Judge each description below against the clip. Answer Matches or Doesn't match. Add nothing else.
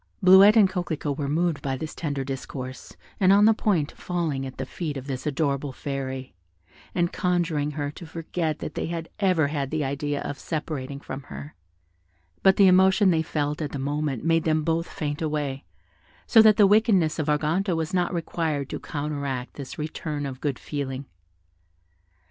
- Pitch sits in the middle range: Matches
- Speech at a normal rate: Matches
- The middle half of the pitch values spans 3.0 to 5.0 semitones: Matches